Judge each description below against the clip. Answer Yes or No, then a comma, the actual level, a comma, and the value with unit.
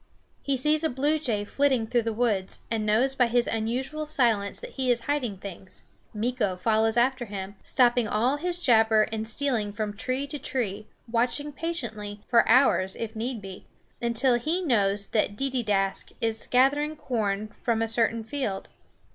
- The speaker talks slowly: No, average, 165 wpm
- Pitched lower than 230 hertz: No, high, 235 Hz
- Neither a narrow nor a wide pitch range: Yes, average, 3.8 semitones